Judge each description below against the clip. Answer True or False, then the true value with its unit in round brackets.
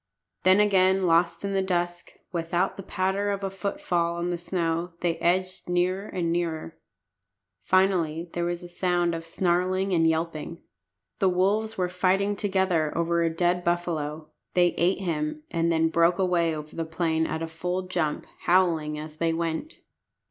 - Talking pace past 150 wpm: True (165 wpm)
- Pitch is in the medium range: True (175 Hz)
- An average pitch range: False (2.1 semitones)